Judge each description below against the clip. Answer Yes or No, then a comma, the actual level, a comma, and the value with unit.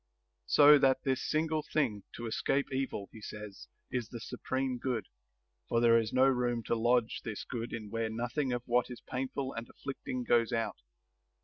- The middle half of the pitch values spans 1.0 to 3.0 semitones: Yes, narrow, 2.5 semitones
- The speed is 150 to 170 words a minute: No, average, 180 wpm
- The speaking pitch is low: Yes, low, 120 Hz